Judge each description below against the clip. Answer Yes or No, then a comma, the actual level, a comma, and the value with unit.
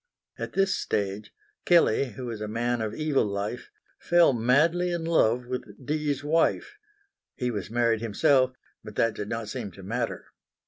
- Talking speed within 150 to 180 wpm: Yes, average, 165 wpm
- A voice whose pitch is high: No, low, 120 Hz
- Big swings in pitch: Yes, wide, 5.7 semitones